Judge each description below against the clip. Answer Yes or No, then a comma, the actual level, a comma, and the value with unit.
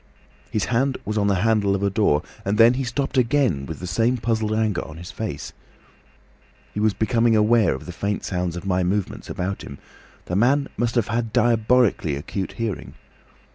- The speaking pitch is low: Yes, low, 110 Hz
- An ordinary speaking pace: Yes, average, 190 wpm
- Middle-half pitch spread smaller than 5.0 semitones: Yes, average, 3.7 semitones